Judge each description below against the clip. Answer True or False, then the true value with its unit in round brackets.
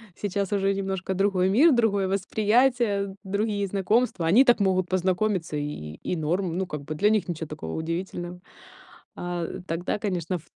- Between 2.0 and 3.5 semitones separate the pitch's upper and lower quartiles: True (2.8 semitones)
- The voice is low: False (190 Hz)